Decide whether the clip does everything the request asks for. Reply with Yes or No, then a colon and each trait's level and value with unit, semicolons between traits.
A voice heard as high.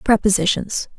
Yes: high, 205 Hz